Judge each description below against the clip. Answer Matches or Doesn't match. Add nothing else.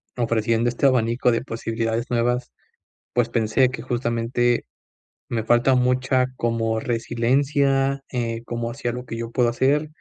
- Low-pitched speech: Matches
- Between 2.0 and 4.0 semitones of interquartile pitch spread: Doesn't match